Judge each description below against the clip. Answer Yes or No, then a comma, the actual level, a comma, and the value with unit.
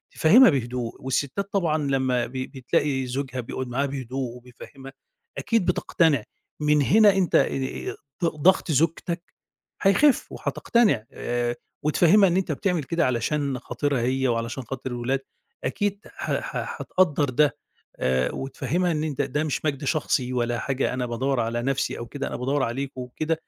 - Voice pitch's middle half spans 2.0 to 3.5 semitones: No, average, 4.0 semitones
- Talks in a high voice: No, low, 135 Hz